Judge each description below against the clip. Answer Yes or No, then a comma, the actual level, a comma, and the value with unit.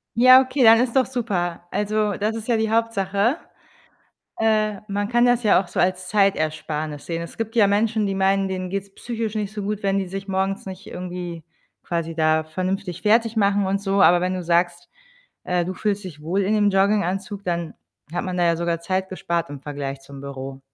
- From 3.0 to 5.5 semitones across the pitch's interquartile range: Yes, average, 3.4 semitones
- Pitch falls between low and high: No, high, 195 Hz